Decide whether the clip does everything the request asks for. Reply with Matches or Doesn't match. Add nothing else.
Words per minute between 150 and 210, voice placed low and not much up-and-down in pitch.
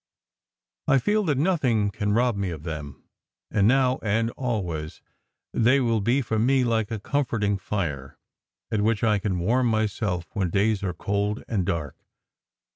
Doesn't match